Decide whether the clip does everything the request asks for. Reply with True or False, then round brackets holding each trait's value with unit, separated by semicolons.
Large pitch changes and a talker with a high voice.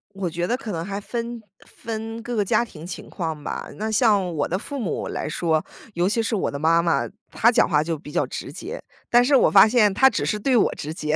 True (5.8 semitones; 200 Hz)